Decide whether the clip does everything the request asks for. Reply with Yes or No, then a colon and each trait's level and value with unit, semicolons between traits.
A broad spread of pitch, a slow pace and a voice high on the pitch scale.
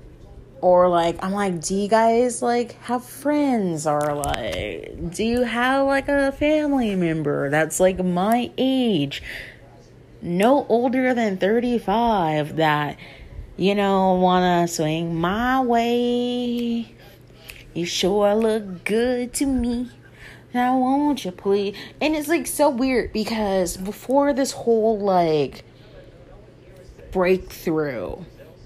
Yes: wide, 6.4 semitones; slow, 115 wpm; high, 205 Hz